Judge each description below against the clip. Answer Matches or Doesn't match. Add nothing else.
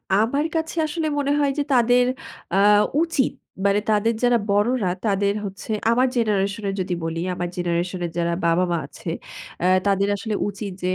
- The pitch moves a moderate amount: Matches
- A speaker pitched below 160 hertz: Doesn't match